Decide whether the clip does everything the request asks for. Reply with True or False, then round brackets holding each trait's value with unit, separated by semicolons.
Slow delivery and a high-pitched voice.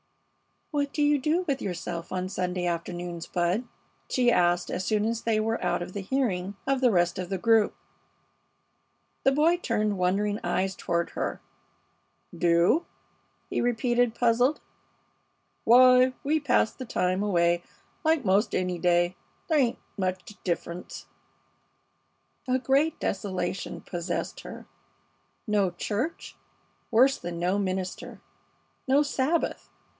True (130 wpm; 205 Hz)